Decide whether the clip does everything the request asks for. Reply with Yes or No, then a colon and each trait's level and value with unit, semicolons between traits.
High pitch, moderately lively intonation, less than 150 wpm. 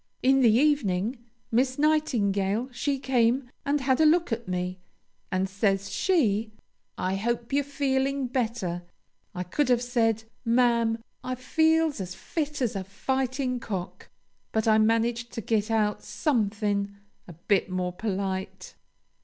Yes: high, 230 Hz; average, 4.8 semitones; average, 140 wpm